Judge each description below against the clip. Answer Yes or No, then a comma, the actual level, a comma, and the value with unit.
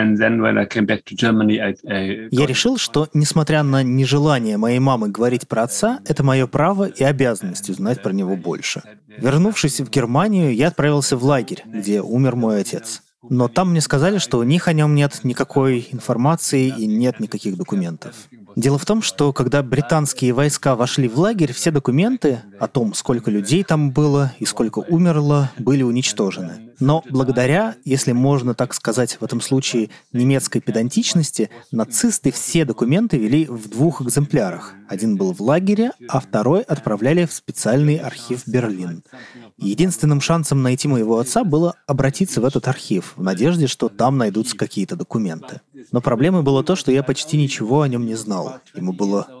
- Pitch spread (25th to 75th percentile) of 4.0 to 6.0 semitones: Yes, average, 4.4 semitones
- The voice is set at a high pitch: No, low, 135 Hz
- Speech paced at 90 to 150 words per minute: No, fast, 160 wpm